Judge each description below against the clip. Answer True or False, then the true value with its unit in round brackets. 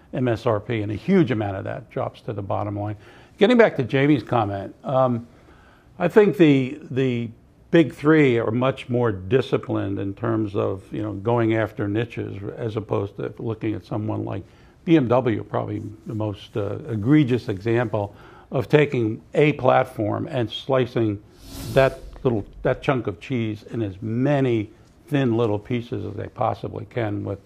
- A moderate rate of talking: True (160 wpm)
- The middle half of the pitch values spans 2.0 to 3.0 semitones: False (3.6 semitones)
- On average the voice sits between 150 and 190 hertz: False (115 Hz)